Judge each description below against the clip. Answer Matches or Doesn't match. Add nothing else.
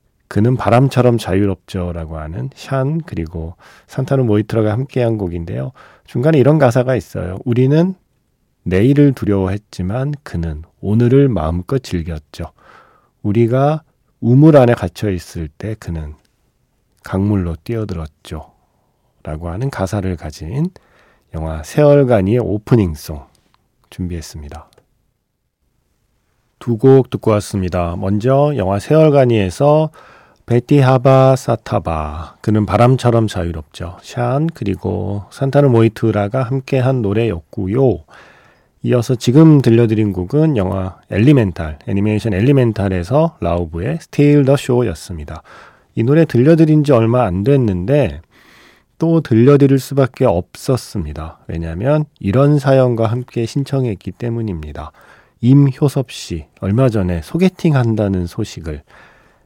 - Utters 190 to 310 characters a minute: Matches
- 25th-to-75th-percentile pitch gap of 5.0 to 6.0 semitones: Doesn't match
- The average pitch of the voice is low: Matches